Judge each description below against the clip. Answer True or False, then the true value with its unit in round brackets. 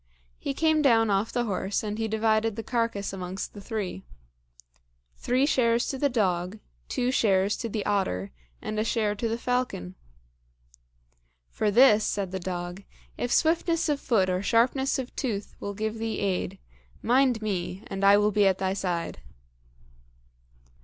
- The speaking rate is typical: True (160 wpm)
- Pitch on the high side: True (215 Hz)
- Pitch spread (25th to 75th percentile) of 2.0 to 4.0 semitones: True (3.7 semitones)